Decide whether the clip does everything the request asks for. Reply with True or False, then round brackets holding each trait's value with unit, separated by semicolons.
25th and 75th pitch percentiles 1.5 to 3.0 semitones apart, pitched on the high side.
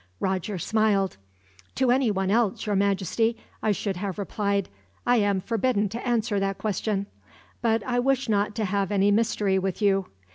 True (2.5 semitones; 205 Hz)